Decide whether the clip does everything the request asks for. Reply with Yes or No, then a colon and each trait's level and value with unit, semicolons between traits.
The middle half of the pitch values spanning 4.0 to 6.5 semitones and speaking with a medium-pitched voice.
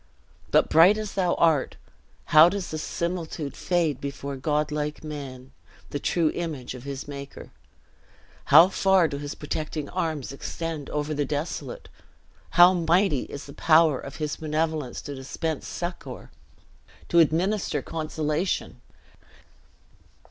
No: average, 3.0 semitones; medium, 155 Hz